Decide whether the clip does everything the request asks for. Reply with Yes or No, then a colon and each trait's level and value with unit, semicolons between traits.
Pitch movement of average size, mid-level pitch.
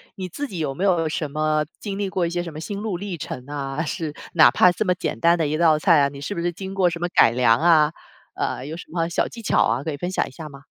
Yes: average, 3.3 semitones; medium, 165 Hz